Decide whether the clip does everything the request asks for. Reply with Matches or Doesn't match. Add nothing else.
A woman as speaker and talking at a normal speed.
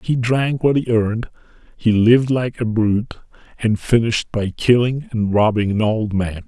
Doesn't match